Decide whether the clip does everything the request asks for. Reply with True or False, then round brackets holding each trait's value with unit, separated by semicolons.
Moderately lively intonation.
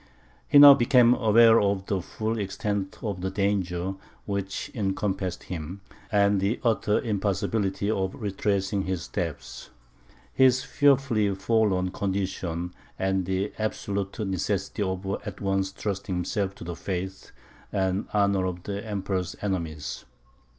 False (1.8 semitones)